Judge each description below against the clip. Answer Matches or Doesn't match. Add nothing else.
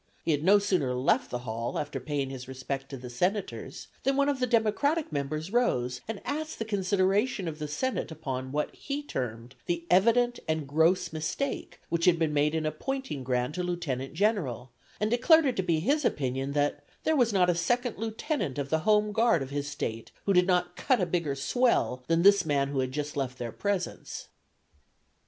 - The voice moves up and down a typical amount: Doesn't match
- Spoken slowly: Doesn't match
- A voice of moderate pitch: Matches